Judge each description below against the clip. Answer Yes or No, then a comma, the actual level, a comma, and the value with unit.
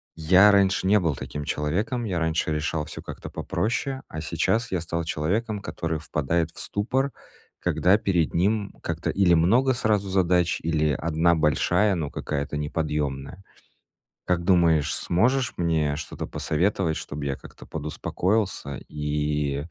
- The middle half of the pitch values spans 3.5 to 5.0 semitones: Yes, average, 4.6 semitones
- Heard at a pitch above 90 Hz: No, very low, 85 Hz